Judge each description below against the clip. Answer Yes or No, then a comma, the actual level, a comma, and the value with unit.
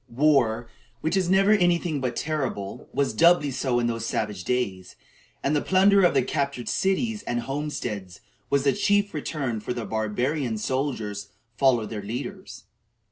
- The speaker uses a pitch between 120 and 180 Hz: Yes, low, 135 Hz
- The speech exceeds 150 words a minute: Yes, average, 165 wpm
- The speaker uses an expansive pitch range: Yes, wide, 5.8 semitones